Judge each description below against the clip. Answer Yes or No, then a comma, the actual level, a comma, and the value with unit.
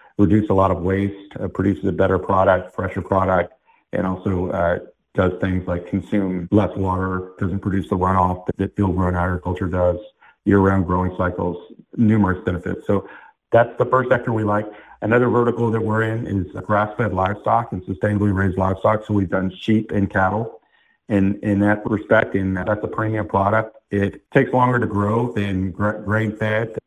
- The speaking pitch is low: Yes, low, 100 Hz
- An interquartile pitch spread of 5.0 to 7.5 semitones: No, narrow, 2.4 semitones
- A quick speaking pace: No, average, 175 wpm